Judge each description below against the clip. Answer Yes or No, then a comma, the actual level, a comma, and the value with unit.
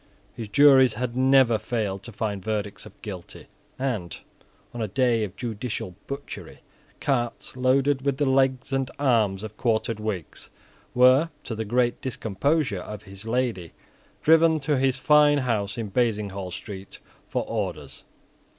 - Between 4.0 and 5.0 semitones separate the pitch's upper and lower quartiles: Yes, average, 4.3 semitones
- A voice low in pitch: Yes, low, 120 Hz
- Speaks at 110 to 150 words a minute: Yes, average, 145 wpm